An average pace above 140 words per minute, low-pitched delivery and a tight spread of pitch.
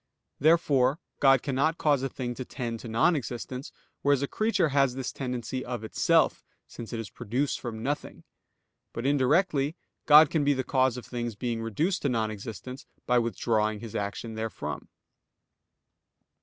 No: average, 160 wpm; low, 125 Hz; average, 3.6 semitones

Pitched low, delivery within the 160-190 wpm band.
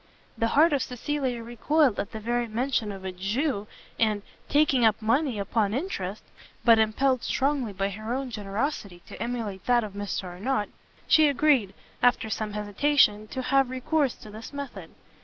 No: high, 230 Hz; average, 165 wpm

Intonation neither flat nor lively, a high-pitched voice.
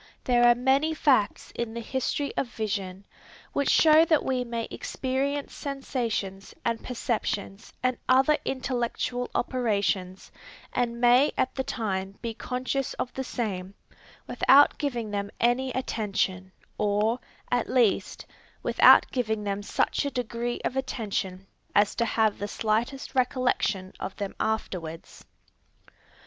Yes: average, 4.0 semitones; high, 235 Hz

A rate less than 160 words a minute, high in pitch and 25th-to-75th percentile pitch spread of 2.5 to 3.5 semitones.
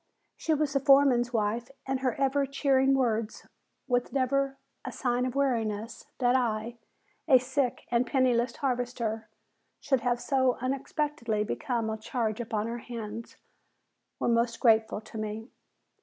Yes: average, 140 wpm; high, 245 Hz; average, 2.9 semitones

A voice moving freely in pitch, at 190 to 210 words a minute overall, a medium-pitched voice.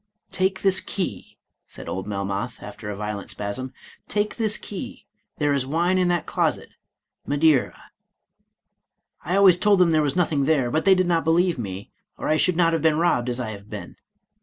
Yes: wide, 6.9 semitones; average, 195 wpm; medium, 155 Hz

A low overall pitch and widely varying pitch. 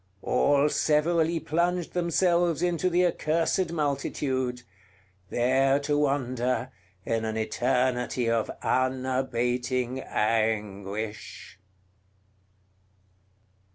No: low, 130 Hz; average, 4.7 semitones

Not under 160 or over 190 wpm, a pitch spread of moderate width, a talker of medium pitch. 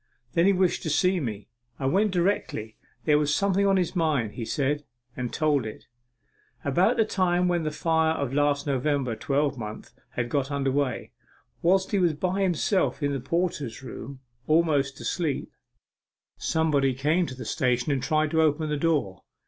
Yes: average, 170 wpm; average, 4.4 semitones; medium, 150 Hz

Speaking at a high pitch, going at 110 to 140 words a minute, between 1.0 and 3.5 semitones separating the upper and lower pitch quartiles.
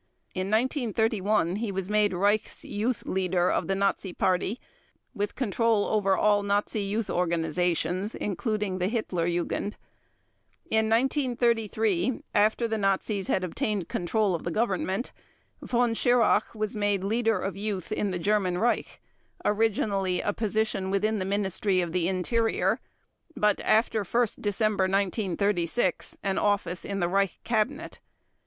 Yes: high, 205 Hz; slow, 135 wpm; average, 2.7 semitones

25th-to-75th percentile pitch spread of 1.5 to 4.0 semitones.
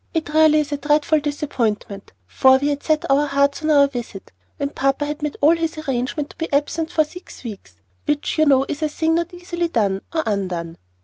Yes: average, 2.9 semitones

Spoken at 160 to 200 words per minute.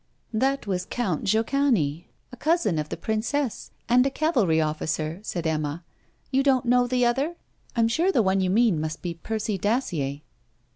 Yes: average, 175 wpm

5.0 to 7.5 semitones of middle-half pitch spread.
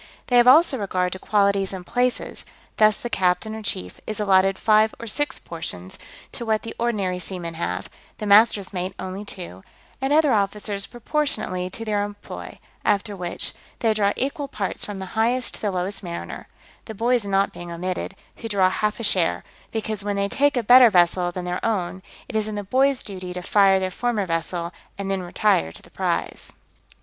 No: average, 3.3 semitones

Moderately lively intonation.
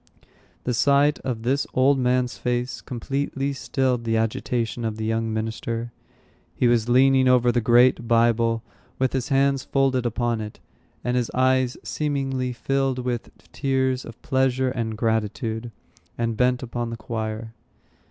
No: narrow, 2.3 semitones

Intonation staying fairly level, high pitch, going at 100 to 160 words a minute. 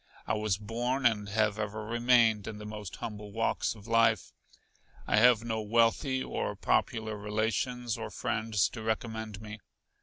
No: narrow, 1.6 semitones; low, 110 Hz; average, 155 wpm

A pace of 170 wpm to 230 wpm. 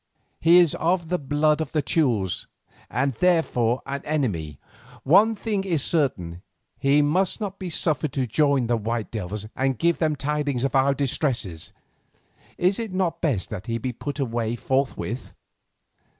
No: average, 160 wpm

